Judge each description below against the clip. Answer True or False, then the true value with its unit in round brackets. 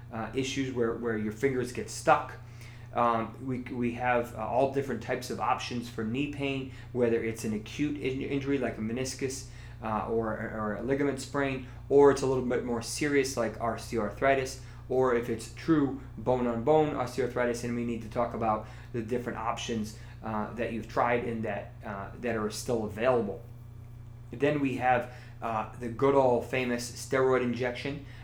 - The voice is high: False (120 Hz)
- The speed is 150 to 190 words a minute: True (180 wpm)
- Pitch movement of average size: False (2.1 semitones)